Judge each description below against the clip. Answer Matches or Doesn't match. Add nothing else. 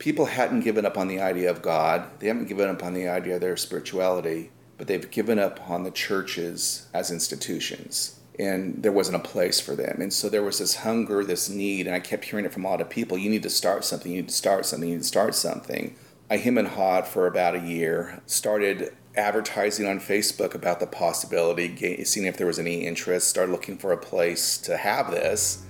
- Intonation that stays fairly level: Matches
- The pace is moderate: Doesn't match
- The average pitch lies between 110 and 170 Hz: Doesn't match